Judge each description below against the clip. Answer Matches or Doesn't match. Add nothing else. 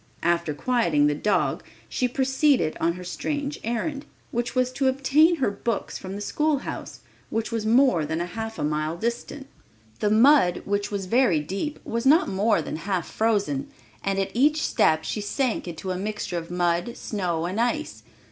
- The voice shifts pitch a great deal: Matches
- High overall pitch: Matches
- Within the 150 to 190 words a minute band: Matches